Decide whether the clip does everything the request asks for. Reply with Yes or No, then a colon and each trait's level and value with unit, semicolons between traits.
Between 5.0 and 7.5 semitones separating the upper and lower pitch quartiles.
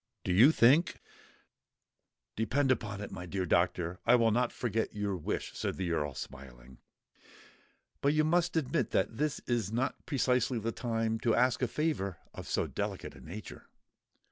Yes: wide, 5.5 semitones